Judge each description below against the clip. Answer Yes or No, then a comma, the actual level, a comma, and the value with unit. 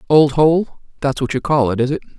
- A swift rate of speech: Yes, fast, 250 wpm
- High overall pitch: No, medium, 140 Hz